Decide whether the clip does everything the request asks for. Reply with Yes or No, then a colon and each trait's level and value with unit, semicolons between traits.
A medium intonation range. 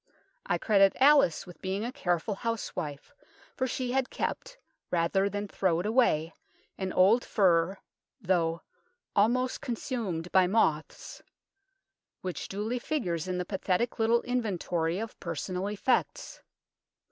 Yes: average, 5.0 semitones